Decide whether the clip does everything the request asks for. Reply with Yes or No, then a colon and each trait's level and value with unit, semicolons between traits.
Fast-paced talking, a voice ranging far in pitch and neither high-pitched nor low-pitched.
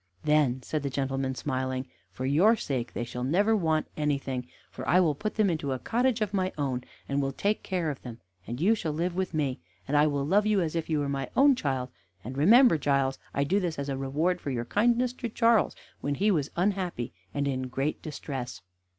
Yes: fast, 220 wpm; wide, 5.8 semitones; medium, 150 Hz